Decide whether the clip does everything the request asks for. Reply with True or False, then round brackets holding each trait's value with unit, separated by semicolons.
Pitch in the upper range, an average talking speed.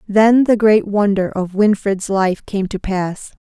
True (200 Hz; 175 wpm)